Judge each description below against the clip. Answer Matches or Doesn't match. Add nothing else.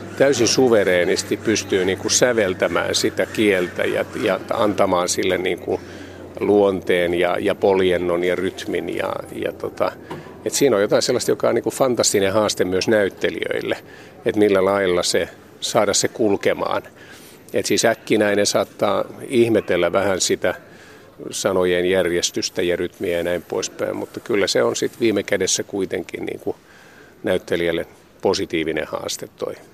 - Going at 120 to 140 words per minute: Matches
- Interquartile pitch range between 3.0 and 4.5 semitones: Doesn't match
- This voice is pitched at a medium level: Doesn't match